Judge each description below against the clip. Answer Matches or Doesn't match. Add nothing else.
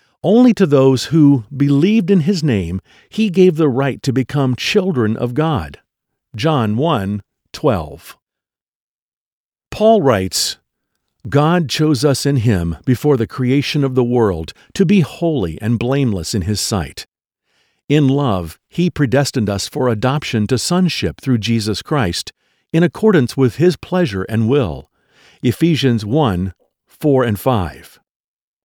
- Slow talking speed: Matches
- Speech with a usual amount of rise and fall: Doesn't match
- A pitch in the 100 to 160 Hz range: Matches